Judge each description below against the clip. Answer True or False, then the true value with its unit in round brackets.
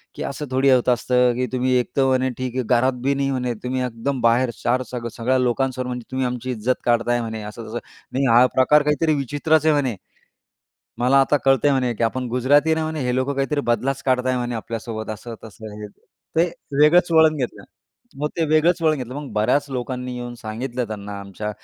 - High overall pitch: False (125 Hz)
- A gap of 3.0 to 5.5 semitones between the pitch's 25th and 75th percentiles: False (2.5 semitones)